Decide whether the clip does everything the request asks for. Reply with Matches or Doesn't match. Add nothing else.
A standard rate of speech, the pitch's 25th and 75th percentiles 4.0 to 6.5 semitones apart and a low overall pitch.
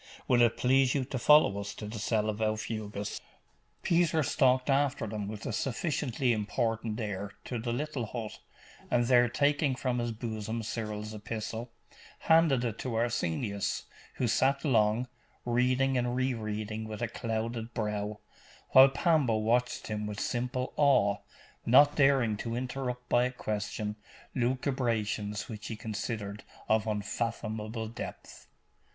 Doesn't match